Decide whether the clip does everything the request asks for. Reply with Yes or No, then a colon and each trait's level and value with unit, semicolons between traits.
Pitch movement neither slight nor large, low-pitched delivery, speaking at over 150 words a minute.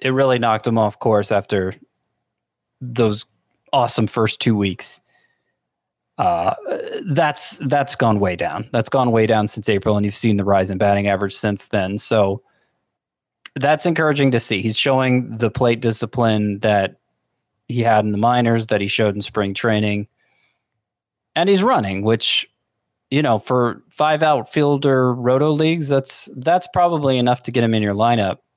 Yes: average, 4.0 semitones; low, 115 Hz; average, 160 wpm